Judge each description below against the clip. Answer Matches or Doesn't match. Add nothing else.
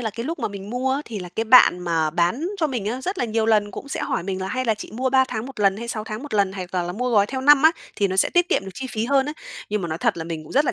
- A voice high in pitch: Matches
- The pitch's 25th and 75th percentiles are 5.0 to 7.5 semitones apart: Matches